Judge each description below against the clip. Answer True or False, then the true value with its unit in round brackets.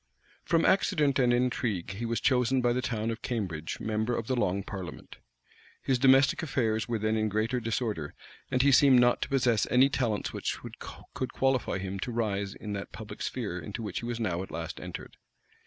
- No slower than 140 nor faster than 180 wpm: False (195 wpm)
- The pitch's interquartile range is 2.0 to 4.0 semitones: True (3.5 semitones)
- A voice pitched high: False (115 Hz)